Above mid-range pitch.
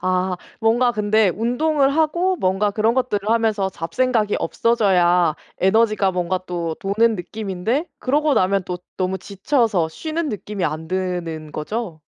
Yes: high, 205 Hz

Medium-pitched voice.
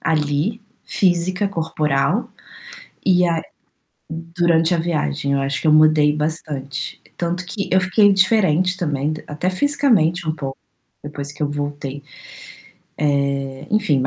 Yes: medium, 160 Hz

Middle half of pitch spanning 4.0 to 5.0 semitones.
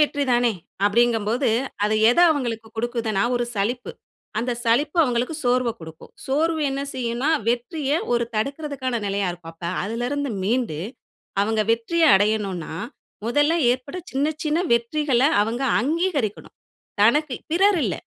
Yes: average, 4.4 semitones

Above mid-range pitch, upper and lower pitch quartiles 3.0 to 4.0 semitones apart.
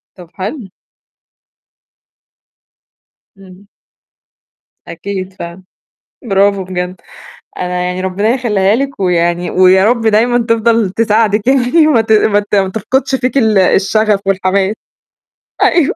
Yes: high, 200 Hz; average, 3.5 semitones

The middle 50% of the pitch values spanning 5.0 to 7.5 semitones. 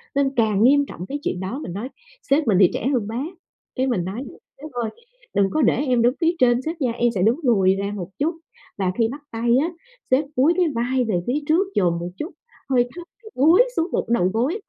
Yes: wide, 5.4 semitones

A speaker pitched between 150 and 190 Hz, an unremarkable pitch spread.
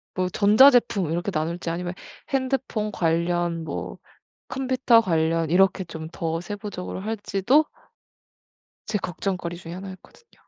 Yes: medium, 185 Hz; average, 4.3 semitones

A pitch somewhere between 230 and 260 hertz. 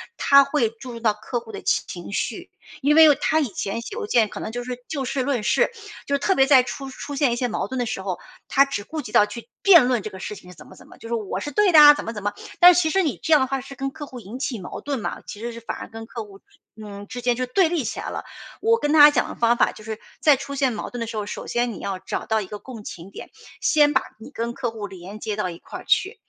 Yes: high, 245 Hz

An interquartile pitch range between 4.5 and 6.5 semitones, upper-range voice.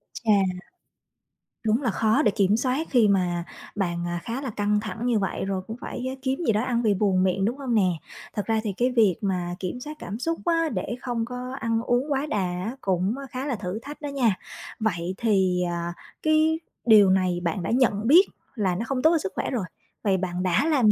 Yes: average, 5.1 semitones; high, 220 Hz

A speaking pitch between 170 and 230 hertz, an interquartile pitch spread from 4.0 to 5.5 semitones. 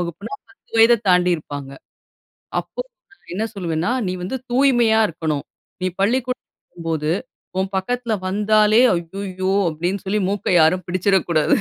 Yes: high, 190 Hz; average, 4.5 semitones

